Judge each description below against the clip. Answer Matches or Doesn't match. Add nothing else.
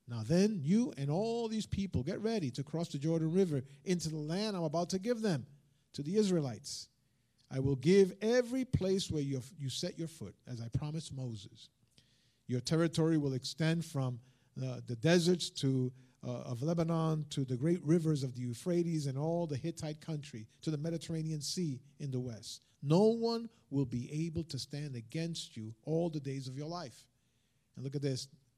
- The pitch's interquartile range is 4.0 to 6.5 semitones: Matches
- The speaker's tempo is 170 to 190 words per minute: Matches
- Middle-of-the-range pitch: Matches